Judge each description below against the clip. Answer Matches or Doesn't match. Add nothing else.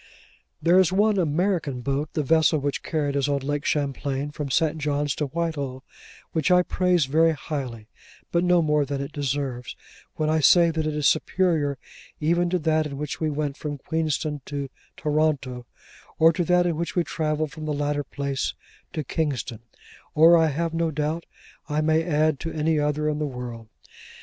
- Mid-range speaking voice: Matches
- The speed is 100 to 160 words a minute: Doesn't match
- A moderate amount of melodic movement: Doesn't match